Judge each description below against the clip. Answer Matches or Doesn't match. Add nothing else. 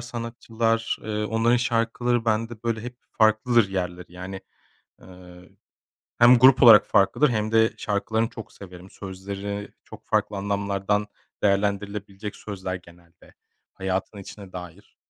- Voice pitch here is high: Doesn't match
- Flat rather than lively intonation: Doesn't match